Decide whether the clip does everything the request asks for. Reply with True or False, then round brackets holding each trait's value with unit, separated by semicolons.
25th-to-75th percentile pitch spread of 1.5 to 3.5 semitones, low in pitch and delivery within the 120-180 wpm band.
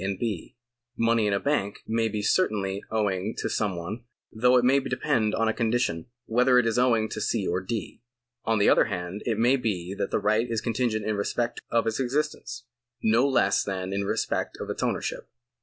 False (3.2 semitones; 110 Hz; 205 wpm)